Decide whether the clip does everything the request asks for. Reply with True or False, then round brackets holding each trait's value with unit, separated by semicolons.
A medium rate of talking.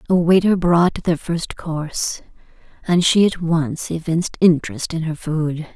True (155 wpm)